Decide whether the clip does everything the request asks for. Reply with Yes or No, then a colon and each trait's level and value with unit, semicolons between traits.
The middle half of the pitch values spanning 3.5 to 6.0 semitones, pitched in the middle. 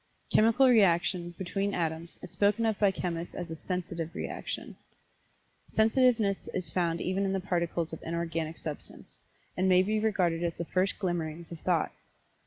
No: average, 2.9 semitones; medium, 180 Hz